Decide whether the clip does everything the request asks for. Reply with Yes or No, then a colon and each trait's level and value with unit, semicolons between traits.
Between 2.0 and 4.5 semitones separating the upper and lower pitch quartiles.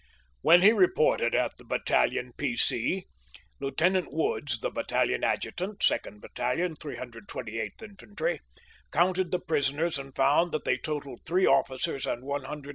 No: average, 5.1 semitones